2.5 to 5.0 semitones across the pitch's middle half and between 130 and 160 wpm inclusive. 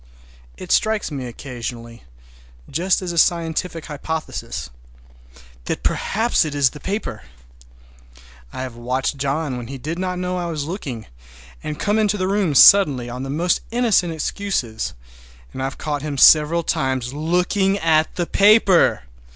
No: wide, 5.6 semitones; average, 150 wpm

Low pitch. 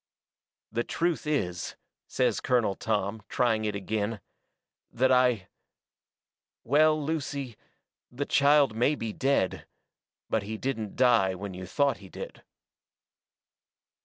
Yes: low, 115 Hz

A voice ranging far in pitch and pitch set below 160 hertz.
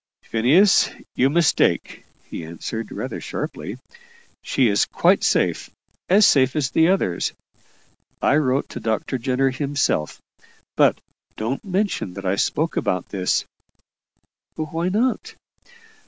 Yes: wide, 6.8 semitones; low, 135 Hz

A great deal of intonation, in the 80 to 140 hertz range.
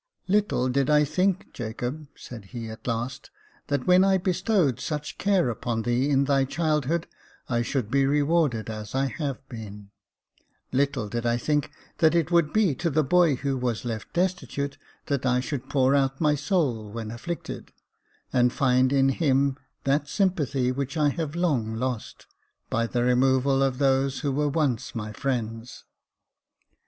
No: average, 3.7 semitones; low, 135 Hz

